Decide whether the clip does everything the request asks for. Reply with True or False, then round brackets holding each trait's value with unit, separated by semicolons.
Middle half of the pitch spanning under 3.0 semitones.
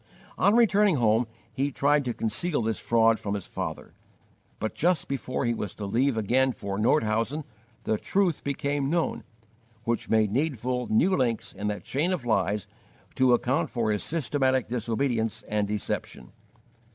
False (4.5 semitones)